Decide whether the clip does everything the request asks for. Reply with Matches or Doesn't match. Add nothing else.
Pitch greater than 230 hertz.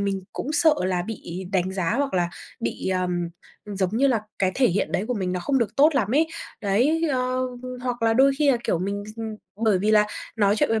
Doesn't match